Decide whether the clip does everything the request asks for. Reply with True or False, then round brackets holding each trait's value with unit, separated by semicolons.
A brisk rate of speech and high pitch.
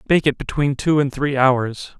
False (210 wpm; 140 Hz)